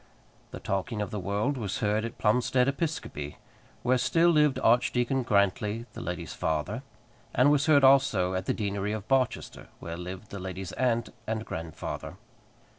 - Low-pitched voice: Yes, low, 110 Hz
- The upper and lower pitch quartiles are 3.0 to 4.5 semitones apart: No, average, 5.0 semitones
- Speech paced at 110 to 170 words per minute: Yes, average, 160 wpm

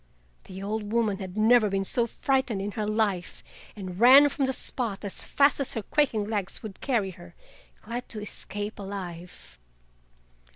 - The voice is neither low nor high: No, high, 210 Hz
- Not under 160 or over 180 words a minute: Yes, average, 165 wpm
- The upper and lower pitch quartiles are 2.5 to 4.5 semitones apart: Yes, average, 3.5 semitones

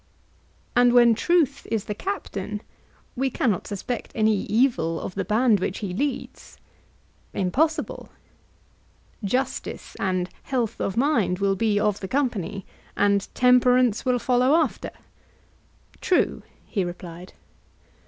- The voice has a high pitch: Yes, high, 220 Hz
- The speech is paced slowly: Yes, slow, 120 wpm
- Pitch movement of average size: Yes, average, 4.6 semitones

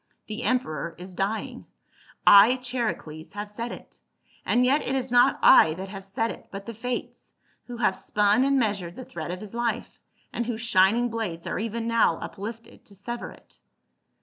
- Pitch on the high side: Yes, high, 220 Hz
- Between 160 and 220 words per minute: Yes, average, 180 wpm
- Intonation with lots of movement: No, average, 3.8 semitones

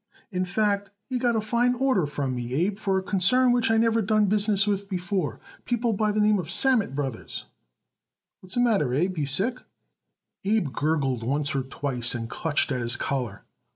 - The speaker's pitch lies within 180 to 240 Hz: Yes, high, 190 Hz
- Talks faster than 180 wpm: Yes, average, 190 wpm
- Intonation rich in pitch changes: Yes, wide, 7.5 semitones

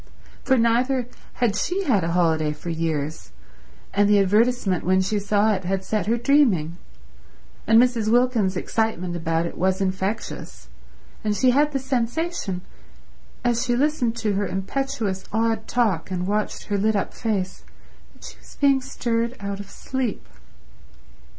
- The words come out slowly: No, average, 155 wpm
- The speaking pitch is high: Yes, high, 215 Hz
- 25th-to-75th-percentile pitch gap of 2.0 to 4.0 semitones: No, average, 4.5 semitones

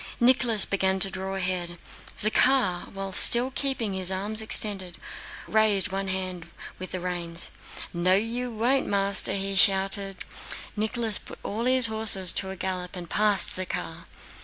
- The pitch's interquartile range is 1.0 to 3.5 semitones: Yes, average, 2.8 semitones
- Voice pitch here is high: Yes, high, 195 Hz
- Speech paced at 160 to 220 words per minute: No, average, 145 wpm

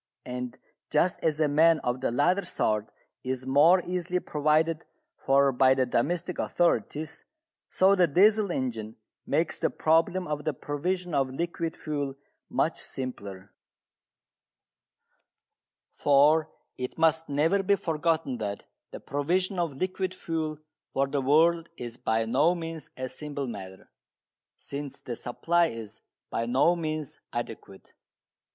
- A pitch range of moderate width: Yes, average, 4.6 semitones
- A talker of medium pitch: Yes, medium, 150 Hz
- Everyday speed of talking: No, slow, 130 wpm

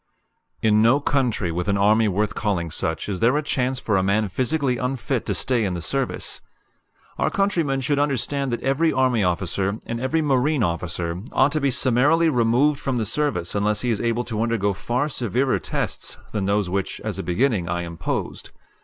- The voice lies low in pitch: Yes, low, 115 Hz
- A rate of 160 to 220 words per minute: Yes, average, 190 wpm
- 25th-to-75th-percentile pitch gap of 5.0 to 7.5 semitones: Yes, average, 5.3 semitones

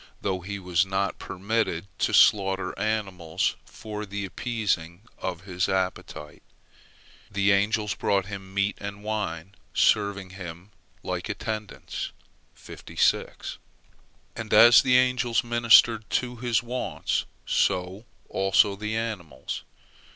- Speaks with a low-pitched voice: Yes, low, 100 Hz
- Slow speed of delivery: Yes, slow, 110 wpm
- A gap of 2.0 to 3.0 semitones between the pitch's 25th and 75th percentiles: Yes, average, 2.7 semitones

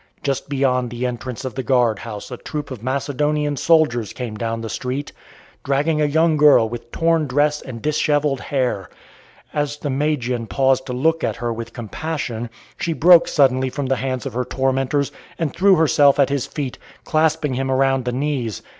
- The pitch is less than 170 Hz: Yes, low, 135 Hz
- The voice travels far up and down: No, average, 3.1 semitones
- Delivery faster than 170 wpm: Yes, average, 180 wpm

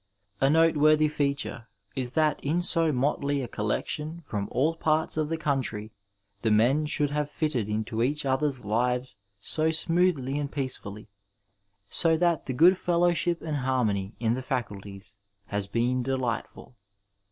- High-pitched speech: No, medium, 140 Hz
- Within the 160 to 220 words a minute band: No, average, 145 wpm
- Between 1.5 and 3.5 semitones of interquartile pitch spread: No, average, 4.8 semitones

